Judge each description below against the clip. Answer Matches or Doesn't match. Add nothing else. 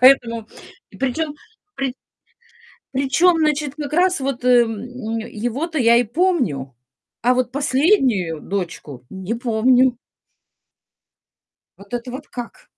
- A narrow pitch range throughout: Doesn't match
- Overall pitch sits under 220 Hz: Doesn't match